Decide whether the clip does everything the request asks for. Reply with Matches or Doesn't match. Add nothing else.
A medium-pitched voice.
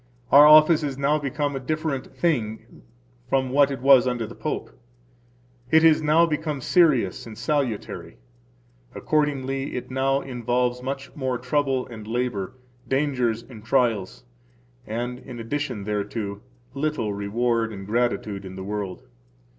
Doesn't match